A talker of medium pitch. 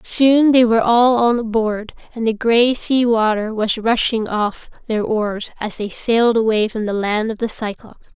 No: high, 225 Hz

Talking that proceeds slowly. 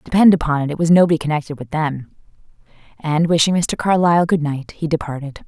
No: average, 185 wpm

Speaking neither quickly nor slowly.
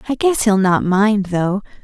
Yes: average, 195 wpm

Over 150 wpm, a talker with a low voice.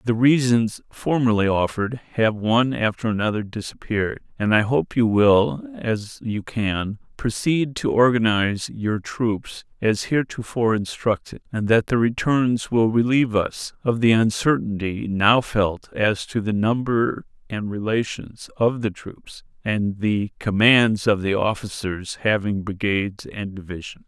No: average, 140 wpm; low, 110 Hz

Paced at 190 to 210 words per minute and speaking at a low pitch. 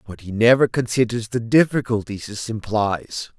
No: average, 140 wpm; low, 115 Hz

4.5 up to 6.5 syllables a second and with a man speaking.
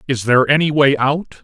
Yes: 5.5 syllables/s; male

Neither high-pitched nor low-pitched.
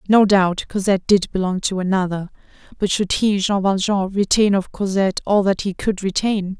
No: high, 195 Hz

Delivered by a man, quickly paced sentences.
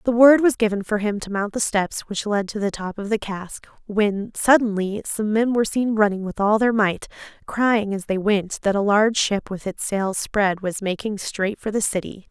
No: female; fast, 230 wpm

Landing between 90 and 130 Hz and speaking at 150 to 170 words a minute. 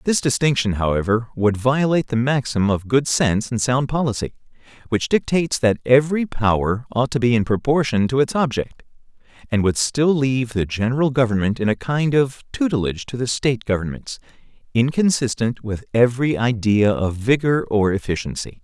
Yes: low, 125 Hz; average, 160 wpm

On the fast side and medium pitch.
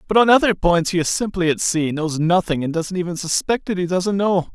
Yes: fast, 250 wpm; medium, 180 Hz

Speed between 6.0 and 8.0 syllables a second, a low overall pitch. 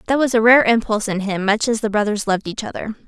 No: 7.0 syllables/s; high, 215 Hz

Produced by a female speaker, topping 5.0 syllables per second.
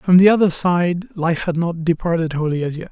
No: male; 5.2 syllables/s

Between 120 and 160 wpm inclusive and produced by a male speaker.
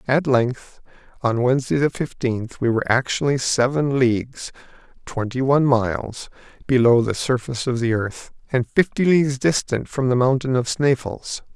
Yes: average, 150 wpm; male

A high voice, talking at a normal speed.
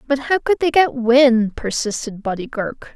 Yes: very high, 250 Hz; average, 185 wpm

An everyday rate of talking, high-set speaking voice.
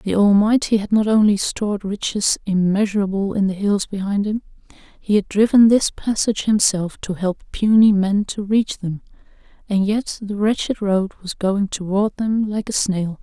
Yes: average, 170 wpm; high, 205 Hz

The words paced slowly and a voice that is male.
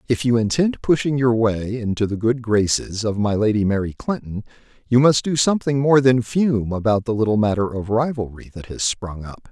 No: average, 200 wpm; male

